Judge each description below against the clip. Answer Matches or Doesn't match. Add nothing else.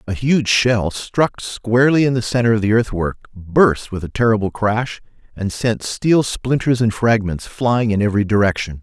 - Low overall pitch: Matches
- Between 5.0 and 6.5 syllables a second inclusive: Doesn't match